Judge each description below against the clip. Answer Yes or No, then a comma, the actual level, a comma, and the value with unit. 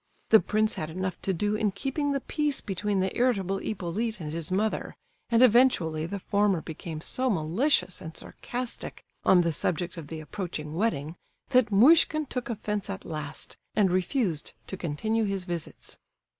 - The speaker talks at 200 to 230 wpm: No, average, 165 wpm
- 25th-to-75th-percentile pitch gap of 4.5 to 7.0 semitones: Yes, average, 5.2 semitones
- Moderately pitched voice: No, high, 195 Hz